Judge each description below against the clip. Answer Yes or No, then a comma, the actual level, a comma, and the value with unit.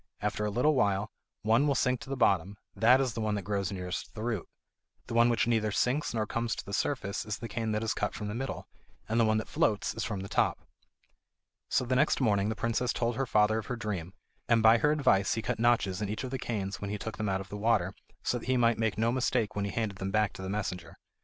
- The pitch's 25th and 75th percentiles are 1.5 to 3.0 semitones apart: Yes, average, 2.7 semitones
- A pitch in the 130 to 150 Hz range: No, low, 110 Hz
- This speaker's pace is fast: Yes, fast, 265 wpm